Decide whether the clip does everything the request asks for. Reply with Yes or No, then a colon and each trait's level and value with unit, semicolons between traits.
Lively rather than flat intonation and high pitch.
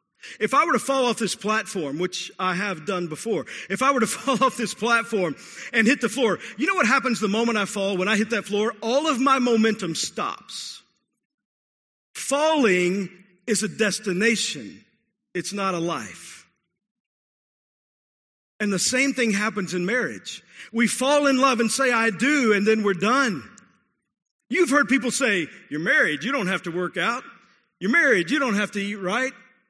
No: average, 4.6 semitones; high, 225 Hz